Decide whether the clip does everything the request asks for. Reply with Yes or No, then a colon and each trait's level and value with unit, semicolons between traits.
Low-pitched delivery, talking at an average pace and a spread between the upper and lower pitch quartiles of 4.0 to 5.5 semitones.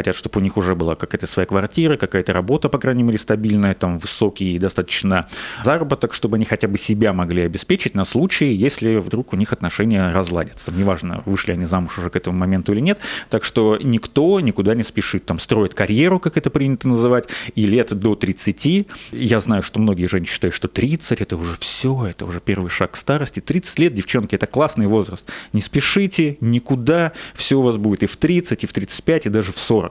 No: low, 110 Hz; fast, 205 wpm; average, 4.6 semitones